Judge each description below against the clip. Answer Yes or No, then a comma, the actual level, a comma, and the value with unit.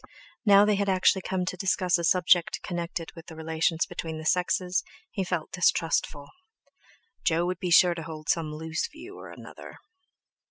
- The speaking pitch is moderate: Yes, medium, 175 Hz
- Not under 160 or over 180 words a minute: Yes, average, 170 wpm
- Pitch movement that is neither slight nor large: No, narrow, 2.3 semitones